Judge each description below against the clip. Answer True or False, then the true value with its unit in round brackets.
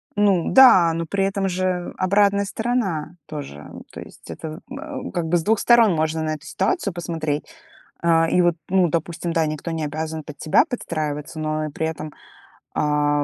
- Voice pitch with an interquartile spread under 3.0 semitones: False (3.9 semitones)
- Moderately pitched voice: True (165 Hz)